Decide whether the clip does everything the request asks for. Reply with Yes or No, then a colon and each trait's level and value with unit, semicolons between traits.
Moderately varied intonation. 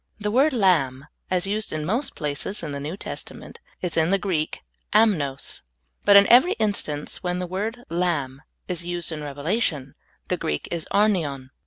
No: wide, 5.7 semitones